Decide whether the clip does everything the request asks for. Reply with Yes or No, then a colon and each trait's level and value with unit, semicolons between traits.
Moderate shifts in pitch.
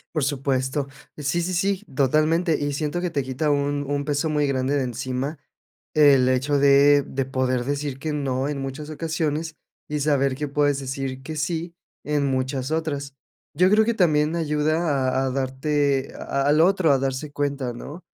No: narrow, 2.3 semitones